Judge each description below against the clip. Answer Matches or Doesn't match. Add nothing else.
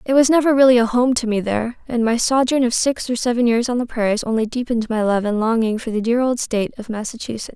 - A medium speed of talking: Doesn't match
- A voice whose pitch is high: Matches